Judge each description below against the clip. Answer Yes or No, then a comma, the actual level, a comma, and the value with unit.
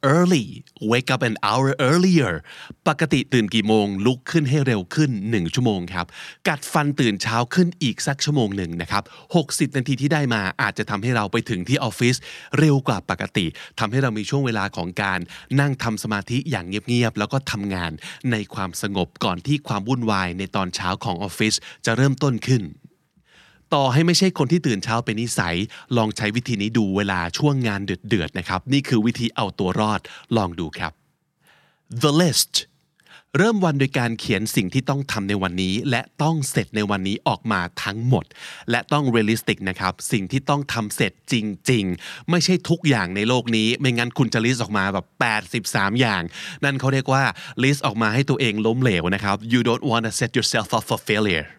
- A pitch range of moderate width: Yes, average, 4.7 semitones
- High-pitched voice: No, low, 115 Hz